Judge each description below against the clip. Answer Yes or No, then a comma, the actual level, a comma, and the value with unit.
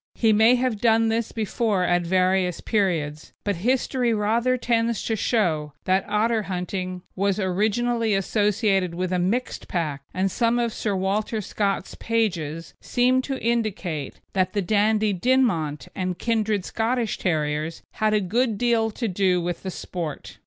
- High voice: Yes, high, 205 Hz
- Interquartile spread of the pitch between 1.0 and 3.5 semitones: No, average, 3.9 semitones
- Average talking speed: Yes, average, 150 wpm